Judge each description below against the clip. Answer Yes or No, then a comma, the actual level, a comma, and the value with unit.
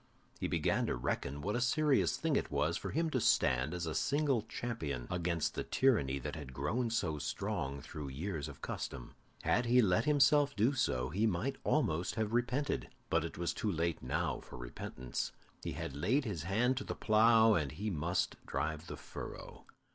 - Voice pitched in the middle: No, very low, 90 Hz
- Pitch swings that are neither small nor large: No, wide, 8.7 semitones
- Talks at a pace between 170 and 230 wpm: Yes, average, 190 wpm